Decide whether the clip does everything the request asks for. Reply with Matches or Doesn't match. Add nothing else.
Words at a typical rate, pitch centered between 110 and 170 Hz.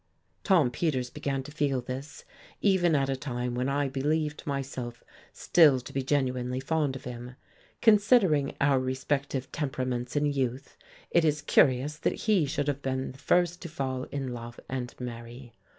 Matches